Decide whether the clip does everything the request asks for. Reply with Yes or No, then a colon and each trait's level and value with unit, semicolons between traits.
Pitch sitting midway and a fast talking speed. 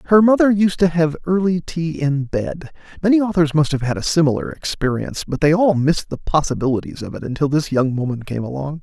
Yes: medium, 155 Hz; fast, 210 wpm